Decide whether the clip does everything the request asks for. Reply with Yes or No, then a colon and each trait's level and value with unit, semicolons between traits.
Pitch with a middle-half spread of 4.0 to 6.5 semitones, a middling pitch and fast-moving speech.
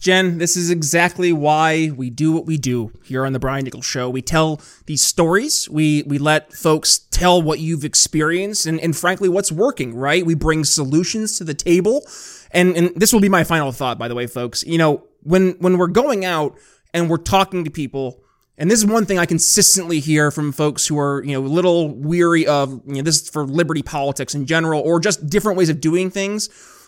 No: average, 3.4 semitones; medium, 160 Hz; fast, 220 wpm